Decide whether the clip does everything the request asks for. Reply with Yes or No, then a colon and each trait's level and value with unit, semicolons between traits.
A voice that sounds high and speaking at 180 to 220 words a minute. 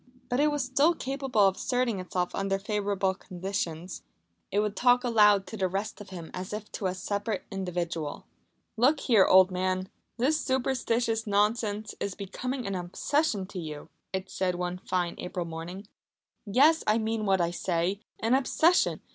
No: high, 200 Hz; average, 165 wpm